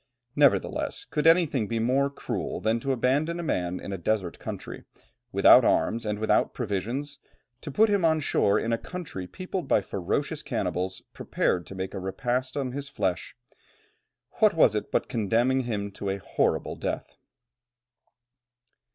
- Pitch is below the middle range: Yes, low, 120 Hz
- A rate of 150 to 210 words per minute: Yes, average, 160 wpm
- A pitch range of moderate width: No, wide, 6.2 semitones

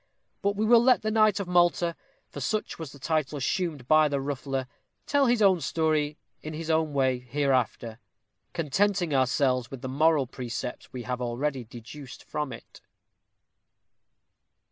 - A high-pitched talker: No, medium, 150 Hz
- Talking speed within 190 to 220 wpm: No, average, 155 wpm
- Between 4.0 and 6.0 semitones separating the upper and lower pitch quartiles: Yes, average, 5.0 semitones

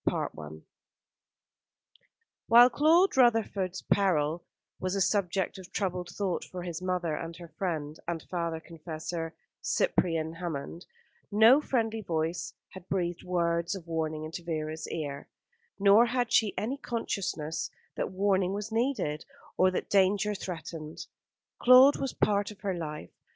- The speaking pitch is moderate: Yes, medium, 180 Hz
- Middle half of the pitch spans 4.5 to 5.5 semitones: No, average, 4.0 semitones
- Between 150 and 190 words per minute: No, average, 140 wpm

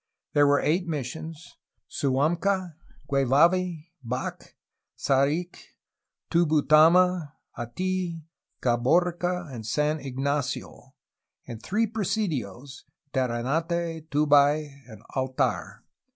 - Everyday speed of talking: No, slow, 85 wpm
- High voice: No, medium, 150 Hz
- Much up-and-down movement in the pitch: No, average, 4.4 semitones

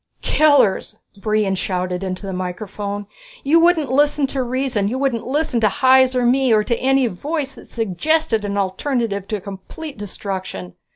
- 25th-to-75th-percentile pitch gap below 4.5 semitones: No, wide, 5.4 semitones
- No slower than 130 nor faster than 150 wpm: No, average, 160 wpm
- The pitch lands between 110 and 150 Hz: No, high, 230 Hz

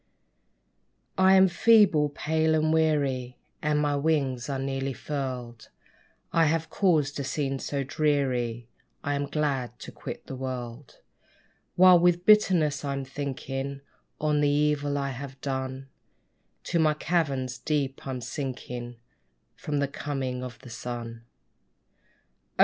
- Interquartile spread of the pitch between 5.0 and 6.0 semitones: No, narrow, 2.6 semitones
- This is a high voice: No, medium, 140 Hz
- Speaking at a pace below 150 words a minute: Yes, slow, 135 wpm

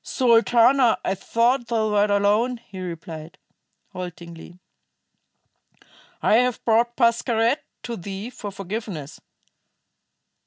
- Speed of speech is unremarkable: No, slow, 95 wpm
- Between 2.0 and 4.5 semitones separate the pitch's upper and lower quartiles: Yes, average, 3.9 semitones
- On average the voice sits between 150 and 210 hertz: No, high, 220 Hz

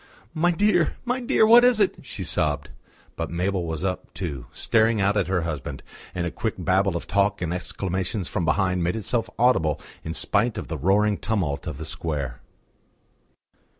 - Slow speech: No, average, 180 wpm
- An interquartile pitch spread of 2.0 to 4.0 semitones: No, average, 5.1 semitones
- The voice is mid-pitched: No, very low, 95 Hz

